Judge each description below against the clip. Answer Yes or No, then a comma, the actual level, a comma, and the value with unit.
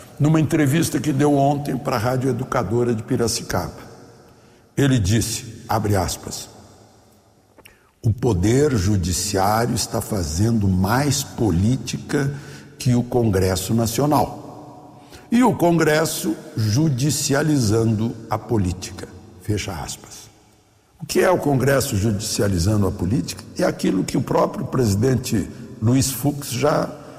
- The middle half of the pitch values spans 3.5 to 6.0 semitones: Yes, average, 5.0 semitones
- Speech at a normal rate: No, slow, 115 wpm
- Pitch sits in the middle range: No, low, 120 Hz